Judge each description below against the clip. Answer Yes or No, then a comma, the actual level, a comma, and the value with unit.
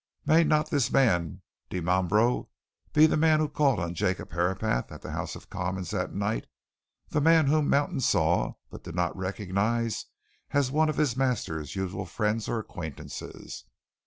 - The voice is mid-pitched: No, low, 110 Hz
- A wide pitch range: Yes, wide, 8.1 semitones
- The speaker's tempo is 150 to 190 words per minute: Yes, average, 160 wpm